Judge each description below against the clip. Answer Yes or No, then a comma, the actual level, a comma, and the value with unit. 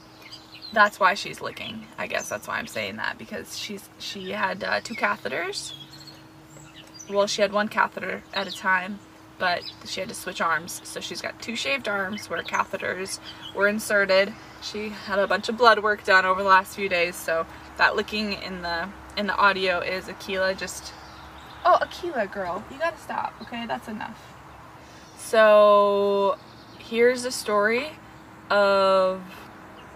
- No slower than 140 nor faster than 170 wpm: Yes, average, 160 wpm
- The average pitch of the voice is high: Yes, high, 200 Hz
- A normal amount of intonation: No, narrow, 2.2 semitones